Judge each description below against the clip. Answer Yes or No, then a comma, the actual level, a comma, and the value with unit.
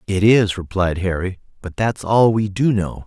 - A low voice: Yes, low, 100 Hz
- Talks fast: No, average, 195 wpm